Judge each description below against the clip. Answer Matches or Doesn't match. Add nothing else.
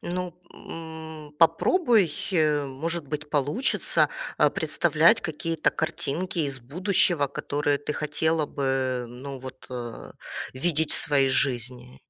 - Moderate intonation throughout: Matches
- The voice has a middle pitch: Matches